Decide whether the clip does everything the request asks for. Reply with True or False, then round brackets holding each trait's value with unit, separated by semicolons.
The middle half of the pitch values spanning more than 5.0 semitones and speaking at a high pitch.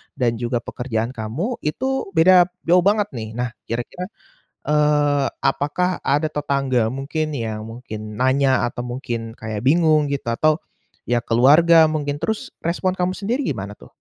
False (5.4 semitones; 140 Hz)